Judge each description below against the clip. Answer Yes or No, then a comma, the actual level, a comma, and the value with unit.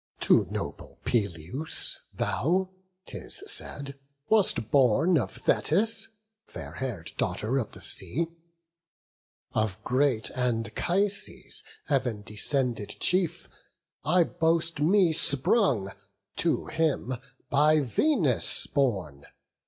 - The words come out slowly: Yes, slow, 95 wpm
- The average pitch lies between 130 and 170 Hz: Yes, medium, 140 Hz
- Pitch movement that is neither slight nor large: No, wide, 7.0 semitones